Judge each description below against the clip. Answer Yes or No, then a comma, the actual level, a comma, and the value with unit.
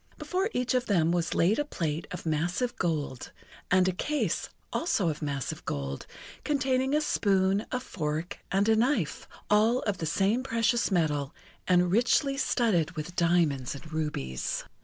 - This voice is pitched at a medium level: Yes, medium, 180 Hz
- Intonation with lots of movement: Yes, wide, 7.2 semitones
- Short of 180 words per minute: Yes, average, 160 wpm